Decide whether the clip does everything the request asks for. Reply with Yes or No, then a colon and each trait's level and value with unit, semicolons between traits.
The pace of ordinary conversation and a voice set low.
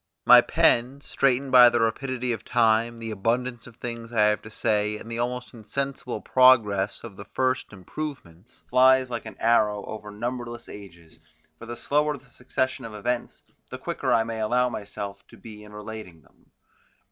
Yes: average, 175 wpm; low, 115 Hz